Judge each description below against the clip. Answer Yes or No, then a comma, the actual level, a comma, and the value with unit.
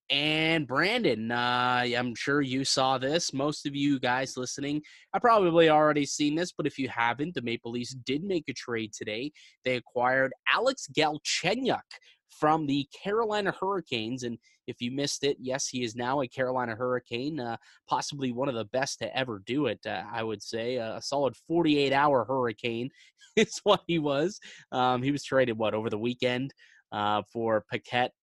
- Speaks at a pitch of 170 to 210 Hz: No, low, 130 Hz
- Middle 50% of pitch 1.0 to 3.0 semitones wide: No, average, 3.5 semitones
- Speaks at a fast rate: No, average, 180 wpm